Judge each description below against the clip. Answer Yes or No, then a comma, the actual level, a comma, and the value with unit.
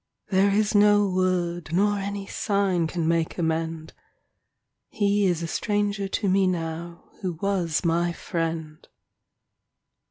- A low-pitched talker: No, medium, 185 Hz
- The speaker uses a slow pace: Yes, slow, 130 wpm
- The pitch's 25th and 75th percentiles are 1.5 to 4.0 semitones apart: Yes, average, 3.3 semitones